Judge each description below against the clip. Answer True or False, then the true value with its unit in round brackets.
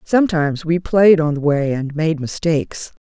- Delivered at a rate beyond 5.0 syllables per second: False (4.9 syllables/s)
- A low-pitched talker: False (160 Hz)